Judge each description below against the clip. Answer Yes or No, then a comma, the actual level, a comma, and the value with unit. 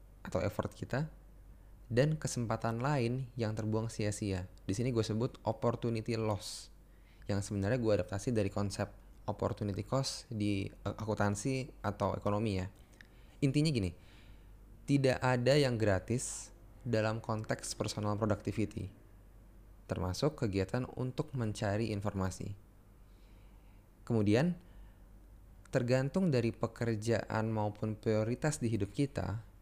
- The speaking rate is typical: Yes, average, 105 wpm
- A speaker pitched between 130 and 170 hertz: No, low, 105 Hz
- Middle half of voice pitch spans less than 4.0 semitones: Yes, average, 2.9 semitones